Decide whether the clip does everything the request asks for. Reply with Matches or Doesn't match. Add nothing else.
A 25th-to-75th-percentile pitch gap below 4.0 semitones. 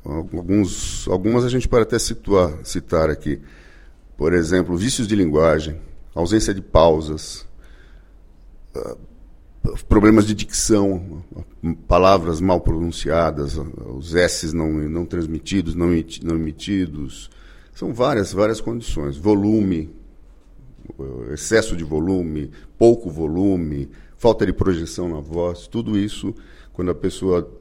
Doesn't match